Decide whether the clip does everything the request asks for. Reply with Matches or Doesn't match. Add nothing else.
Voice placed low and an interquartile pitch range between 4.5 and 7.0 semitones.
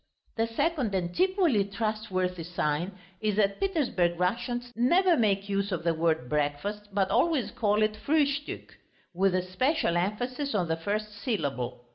Doesn't match